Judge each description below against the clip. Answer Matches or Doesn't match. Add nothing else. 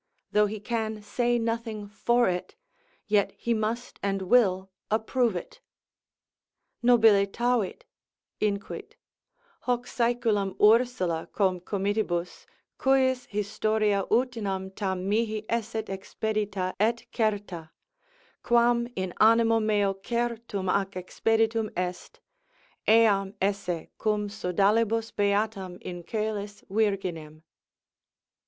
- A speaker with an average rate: Doesn't match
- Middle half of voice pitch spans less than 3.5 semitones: Matches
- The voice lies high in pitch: Matches